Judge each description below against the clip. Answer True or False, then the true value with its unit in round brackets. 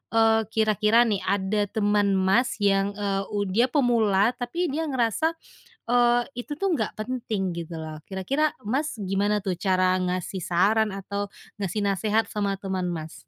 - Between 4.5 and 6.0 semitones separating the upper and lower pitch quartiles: False (3.5 semitones)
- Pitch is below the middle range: False (205 Hz)